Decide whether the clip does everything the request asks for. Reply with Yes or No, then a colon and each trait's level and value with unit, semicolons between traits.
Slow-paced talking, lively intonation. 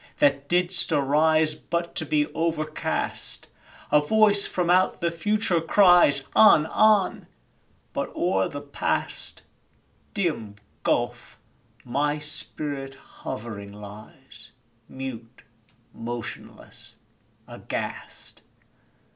No: slow, 90 wpm; average, 4.6 semitones